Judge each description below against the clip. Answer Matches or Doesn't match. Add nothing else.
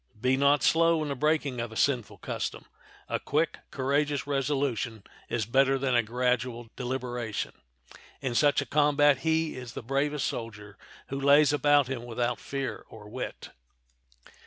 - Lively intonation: Doesn't match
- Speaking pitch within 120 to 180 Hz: Matches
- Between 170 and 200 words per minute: Doesn't match